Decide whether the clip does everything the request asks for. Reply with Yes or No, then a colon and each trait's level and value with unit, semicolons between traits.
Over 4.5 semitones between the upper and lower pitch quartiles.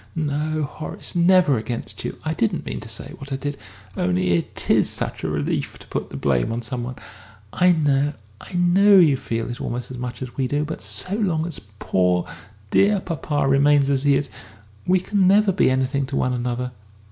Yes: average, 5.1 semitones